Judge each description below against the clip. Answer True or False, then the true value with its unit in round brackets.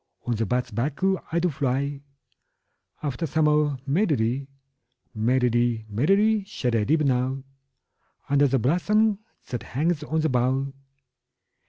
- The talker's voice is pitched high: False (140 Hz)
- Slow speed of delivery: True (130 wpm)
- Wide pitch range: False (4.2 semitones)